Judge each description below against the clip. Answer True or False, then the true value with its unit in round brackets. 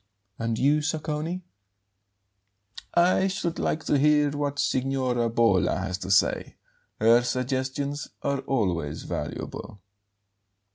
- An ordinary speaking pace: False (105 wpm)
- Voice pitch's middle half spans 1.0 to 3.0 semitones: False (4.5 semitones)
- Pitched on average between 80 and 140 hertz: True (135 Hz)